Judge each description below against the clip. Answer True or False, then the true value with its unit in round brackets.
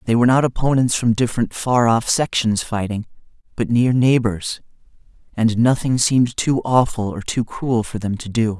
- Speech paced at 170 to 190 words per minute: True (175 wpm)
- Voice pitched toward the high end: False (115 Hz)